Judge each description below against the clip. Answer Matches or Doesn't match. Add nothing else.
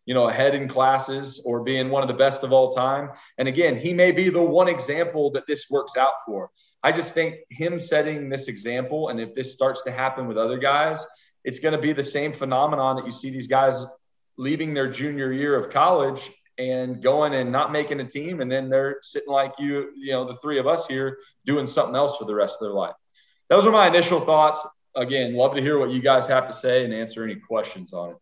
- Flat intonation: Matches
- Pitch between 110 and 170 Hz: Matches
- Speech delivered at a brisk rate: Matches